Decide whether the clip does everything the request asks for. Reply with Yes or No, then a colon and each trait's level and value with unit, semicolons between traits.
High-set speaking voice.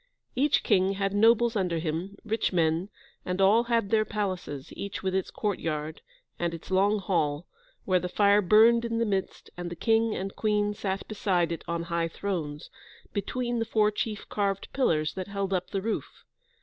Yes: high, 195 Hz